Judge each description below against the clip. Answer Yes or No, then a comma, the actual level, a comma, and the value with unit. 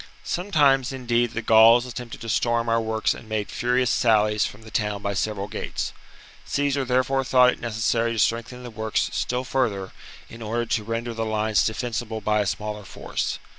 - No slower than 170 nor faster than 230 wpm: Yes, average, 180 wpm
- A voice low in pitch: Yes, low, 115 Hz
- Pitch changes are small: Yes, narrow, 2.2 semitones